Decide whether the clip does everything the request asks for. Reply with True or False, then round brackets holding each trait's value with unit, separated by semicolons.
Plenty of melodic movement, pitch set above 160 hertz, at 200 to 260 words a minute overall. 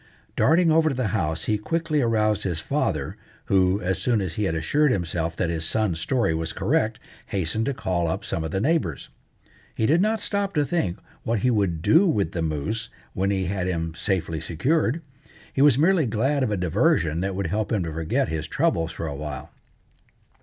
False (8.2 semitones; 100 Hz; 205 wpm)